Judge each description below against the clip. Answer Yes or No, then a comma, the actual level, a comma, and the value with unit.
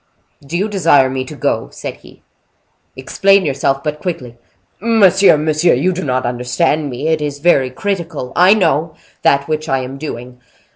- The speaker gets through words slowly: No, average, 150 wpm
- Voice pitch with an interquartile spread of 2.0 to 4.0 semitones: No, average, 5.0 semitones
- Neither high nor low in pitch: Yes, medium, 150 Hz